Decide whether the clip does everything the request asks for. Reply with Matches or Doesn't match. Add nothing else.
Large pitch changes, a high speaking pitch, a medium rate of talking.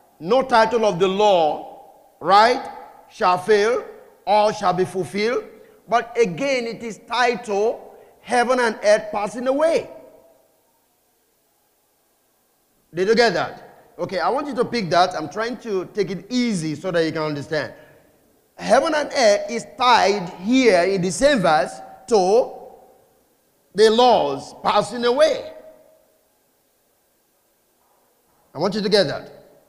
Doesn't match